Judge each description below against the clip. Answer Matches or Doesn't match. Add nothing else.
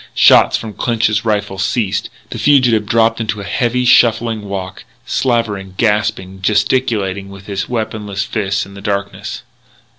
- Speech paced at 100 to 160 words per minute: Matches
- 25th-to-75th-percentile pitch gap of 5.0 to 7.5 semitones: Doesn't match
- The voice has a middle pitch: Doesn't match